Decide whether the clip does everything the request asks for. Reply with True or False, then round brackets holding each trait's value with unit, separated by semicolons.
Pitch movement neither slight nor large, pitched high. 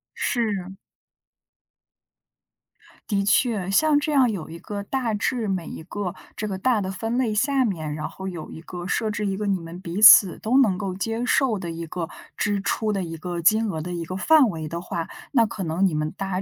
True (4.2 semitones; 195 Hz)